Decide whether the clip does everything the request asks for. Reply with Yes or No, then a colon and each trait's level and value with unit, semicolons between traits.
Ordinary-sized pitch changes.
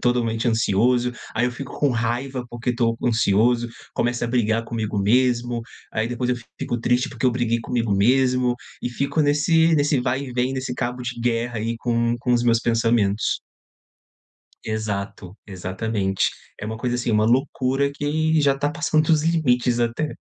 No: narrow, 2.2 semitones